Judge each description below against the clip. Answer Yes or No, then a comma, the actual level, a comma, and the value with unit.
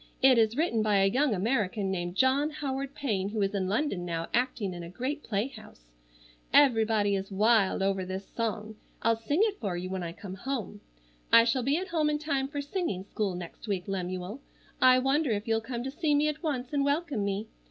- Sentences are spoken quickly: Yes, fast, 210 wpm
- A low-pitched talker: No, high, 225 Hz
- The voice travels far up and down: Yes, wide, 6.0 semitones